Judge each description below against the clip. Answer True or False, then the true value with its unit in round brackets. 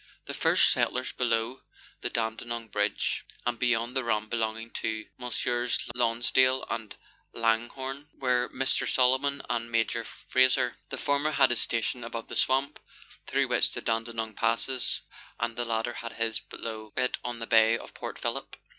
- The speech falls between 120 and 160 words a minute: True (155 wpm)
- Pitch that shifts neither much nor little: False (1.9 semitones)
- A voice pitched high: False (120 Hz)